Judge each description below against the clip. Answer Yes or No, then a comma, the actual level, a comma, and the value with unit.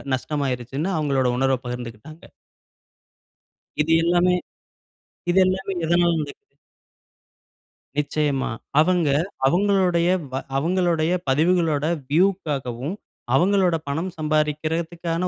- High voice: No, medium, 160 Hz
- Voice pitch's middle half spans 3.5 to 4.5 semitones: Yes, average, 3.8 semitones